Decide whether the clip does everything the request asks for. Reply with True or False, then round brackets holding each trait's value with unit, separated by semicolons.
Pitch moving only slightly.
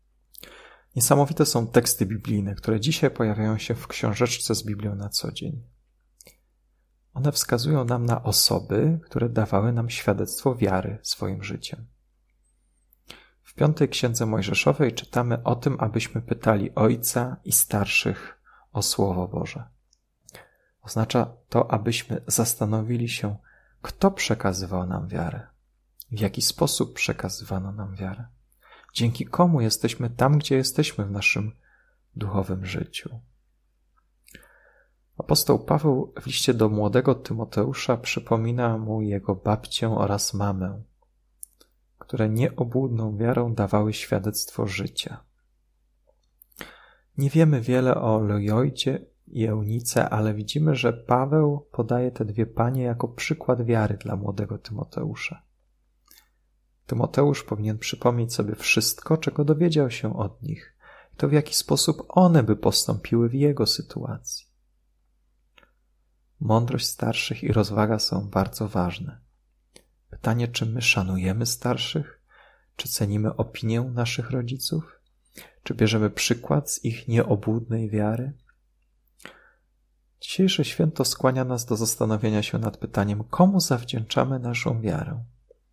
False (3.9 semitones)